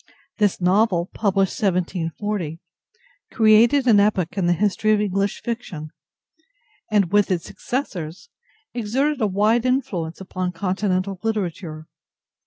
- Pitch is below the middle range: No, high, 200 Hz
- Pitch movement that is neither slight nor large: Yes, average, 3.3 semitones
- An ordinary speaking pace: No, slow, 115 wpm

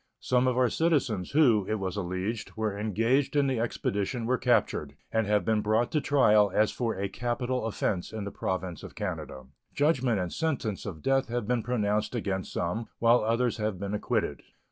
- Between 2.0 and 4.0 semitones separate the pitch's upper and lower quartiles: Yes, average, 3.5 semitones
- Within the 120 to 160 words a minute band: No, average, 190 wpm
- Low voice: Yes, low, 110 Hz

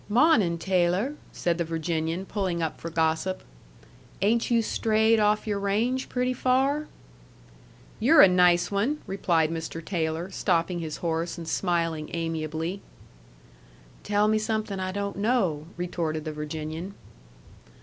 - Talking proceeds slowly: Yes, slow, 130 wpm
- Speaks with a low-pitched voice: No, medium, 180 Hz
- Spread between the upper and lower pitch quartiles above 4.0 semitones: Yes, average, 4.5 semitones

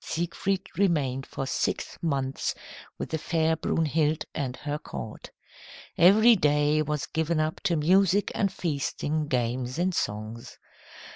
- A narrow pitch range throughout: No, average, 3.9 semitones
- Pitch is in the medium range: Yes, medium, 155 Hz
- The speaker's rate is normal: No, slow, 130 wpm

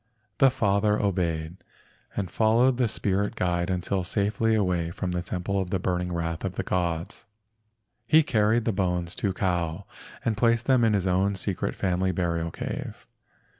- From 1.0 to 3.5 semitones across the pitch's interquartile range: Yes, average, 3.2 semitones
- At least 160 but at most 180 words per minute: Yes, average, 165 wpm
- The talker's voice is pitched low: Yes, very low, 95 Hz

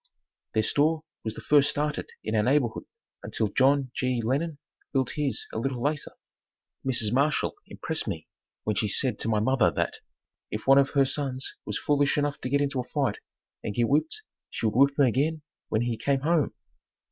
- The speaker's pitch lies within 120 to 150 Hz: Yes, low, 135 Hz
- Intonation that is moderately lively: Yes, average, 3.7 semitones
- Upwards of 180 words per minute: Yes, average, 190 wpm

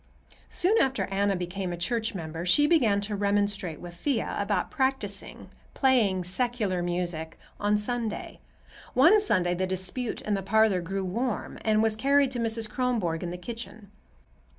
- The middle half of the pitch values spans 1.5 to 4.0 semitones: No, average, 4.8 semitones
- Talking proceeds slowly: No, average, 150 wpm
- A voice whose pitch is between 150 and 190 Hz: No, high, 205 Hz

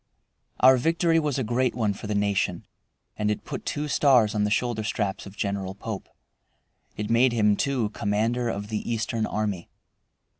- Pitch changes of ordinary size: Yes, average, 3.2 semitones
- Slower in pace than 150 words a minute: No, average, 175 wpm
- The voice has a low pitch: Yes, low, 110 Hz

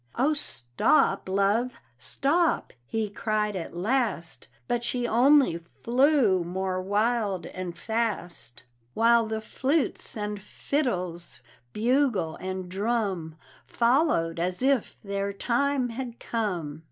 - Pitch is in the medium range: No, high, 215 Hz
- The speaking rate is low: Yes, slow, 110 wpm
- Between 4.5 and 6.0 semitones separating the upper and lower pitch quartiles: Yes, average, 4.9 semitones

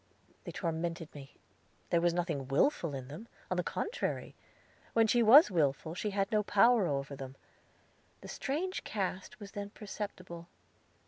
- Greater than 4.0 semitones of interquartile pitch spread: Yes, average, 5.1 semitones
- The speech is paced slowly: No, average, 150 wpm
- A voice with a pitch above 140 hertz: Yes, medium, 185 Hz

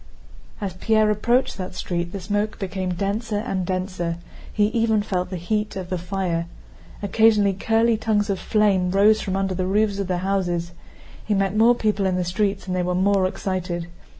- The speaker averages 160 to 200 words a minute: Yes, average, 180 wpm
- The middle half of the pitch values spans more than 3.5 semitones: No, narrow, 2.6 semitones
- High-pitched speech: Yes, high, 195 Hz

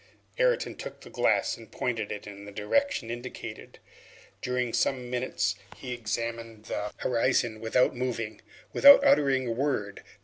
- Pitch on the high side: No, low, 120 Hz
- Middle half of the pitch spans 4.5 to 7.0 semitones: No, average, 2.9 semitones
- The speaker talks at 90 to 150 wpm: Yes, average, 140 wpm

